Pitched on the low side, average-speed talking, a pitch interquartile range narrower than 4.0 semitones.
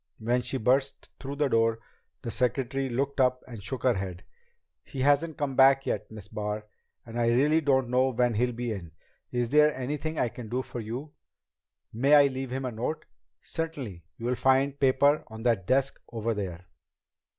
Yes: low, 125 Hz; average, 185 wpm; average, 3.1 semitones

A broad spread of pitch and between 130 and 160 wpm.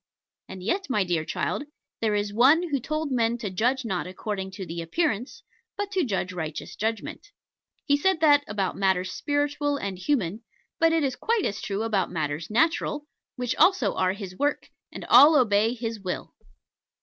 No: wide, 7.3 semitones; average, 175 wpm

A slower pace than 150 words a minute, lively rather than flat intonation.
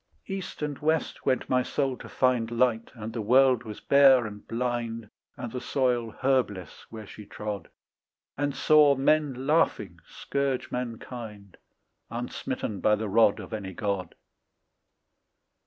No: average, 140 wpm; average, 3.7 semitones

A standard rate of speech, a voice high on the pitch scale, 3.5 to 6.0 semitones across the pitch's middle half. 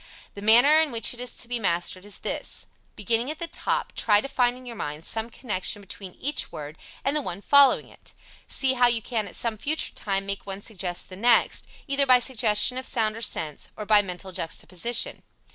No: fast, 210 wpm; high, 225 Hz; average, 4.2 semitones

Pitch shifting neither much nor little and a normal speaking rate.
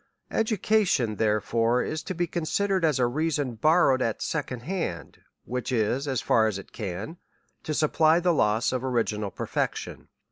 No: wide, 6.3 semitones; average, 150 wpm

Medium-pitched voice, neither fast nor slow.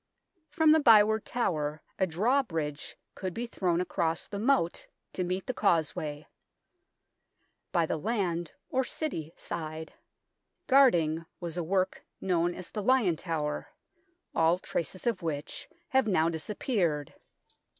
No: medium, 175 Hz; slow, 130 wpm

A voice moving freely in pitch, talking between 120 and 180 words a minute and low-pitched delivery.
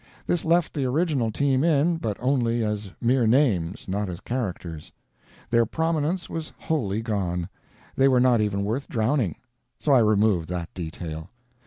Yes: wide, 6.1 semitones; average, 155 wpm; low, 115 Hz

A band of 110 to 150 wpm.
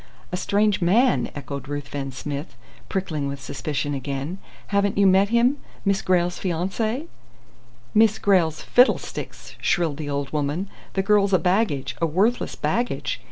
Yes: average, 140 wpm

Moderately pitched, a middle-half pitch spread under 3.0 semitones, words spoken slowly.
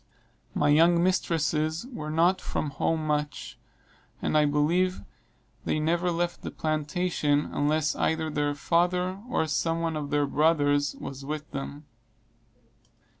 Yes: medium, 155 Hz; narrow, 2.5 semitones; slow, 130 wpm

